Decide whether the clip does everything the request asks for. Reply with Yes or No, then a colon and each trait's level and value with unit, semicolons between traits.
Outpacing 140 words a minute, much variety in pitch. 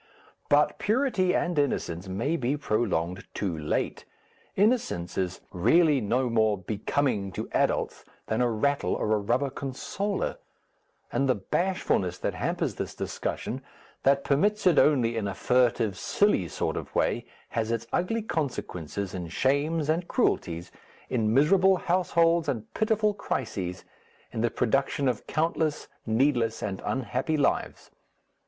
No: slow, 135 wpm; wide, 7.4 semitones